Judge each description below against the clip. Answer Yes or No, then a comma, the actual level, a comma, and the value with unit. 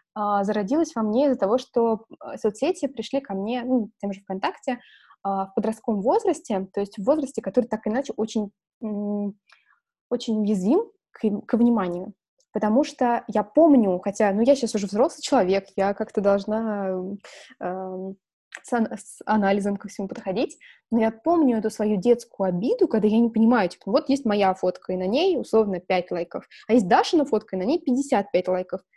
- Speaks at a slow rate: No, fast, 170 wpm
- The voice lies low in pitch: No, high, 220 Hz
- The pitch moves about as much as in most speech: Yes, average, 4.4 semitones